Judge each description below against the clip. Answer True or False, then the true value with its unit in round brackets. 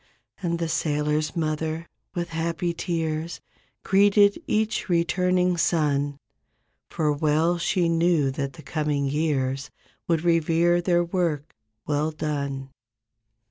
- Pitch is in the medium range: True (160 Hz)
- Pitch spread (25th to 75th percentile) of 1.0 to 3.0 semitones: True (2.5 semitones)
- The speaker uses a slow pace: True (110 wpm)